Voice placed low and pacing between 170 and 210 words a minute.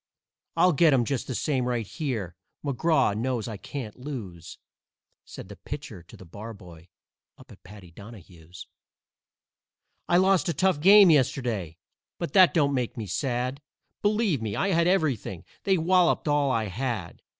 No: low, 130 Hz; average, 155 wpm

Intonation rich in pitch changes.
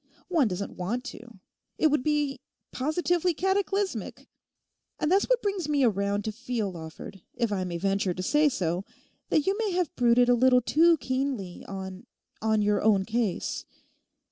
Yes: wide, 7.5 semitones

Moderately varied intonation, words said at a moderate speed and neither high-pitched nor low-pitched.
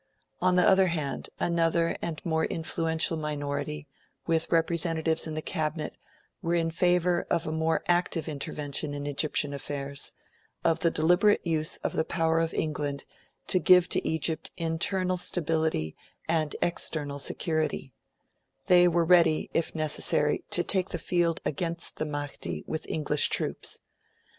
No: narrow, 2.0 semitones; average, 145 wpm; medium, 160 Hz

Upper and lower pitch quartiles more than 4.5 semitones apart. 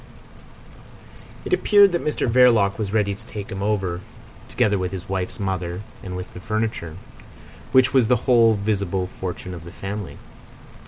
No: average, 3.5 semitones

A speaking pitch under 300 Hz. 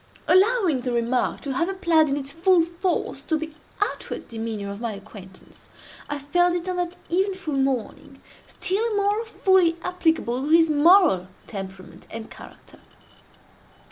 No: very high, 320 Hz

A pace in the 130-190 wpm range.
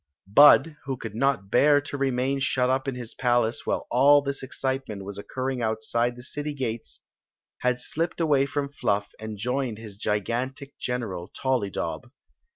Yes: average, 160 wpm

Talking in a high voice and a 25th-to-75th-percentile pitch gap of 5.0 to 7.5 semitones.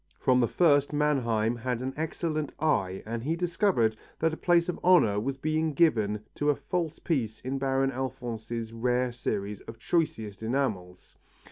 No: low, 130 Hz; wide, 5.4 semitones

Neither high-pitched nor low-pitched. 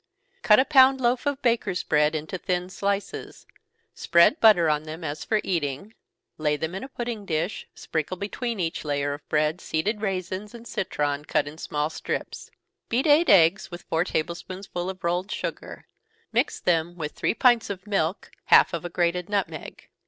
Yes: medium, 180 Hz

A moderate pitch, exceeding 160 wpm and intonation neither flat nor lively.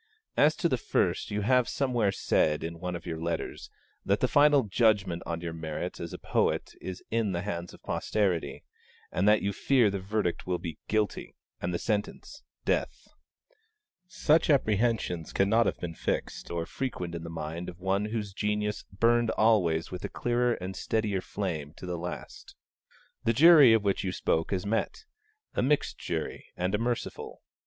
No: low, 100 Hz; average, 180 wpm; average, 4.8 semitones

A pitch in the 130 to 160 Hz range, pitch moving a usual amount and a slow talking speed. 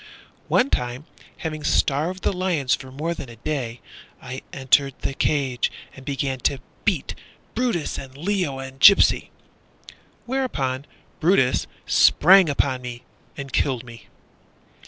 Yes: medium, 140 Hz; average, 4.4 semitones; slow, 130 wpm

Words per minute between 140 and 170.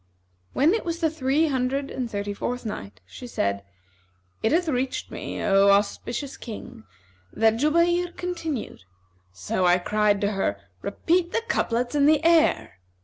Yes: average, 150 wpm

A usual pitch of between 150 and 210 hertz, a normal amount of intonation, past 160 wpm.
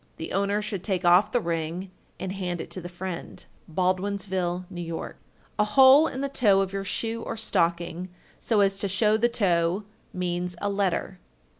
Yes: high, 190 Hz; average, 3.0 semitones; average, 180 wpm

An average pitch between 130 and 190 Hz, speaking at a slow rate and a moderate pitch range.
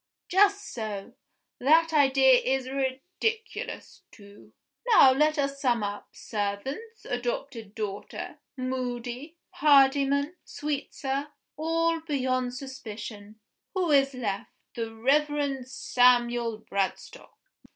No: very high, 265 Hz; slow, 95 wpm; average, 3.7 semitones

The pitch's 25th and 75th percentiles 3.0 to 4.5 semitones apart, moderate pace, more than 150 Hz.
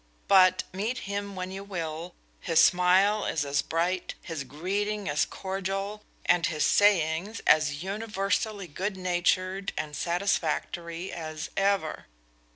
No: average, 3.3 semitones; slow, 125 wpm; medium, 185 Hz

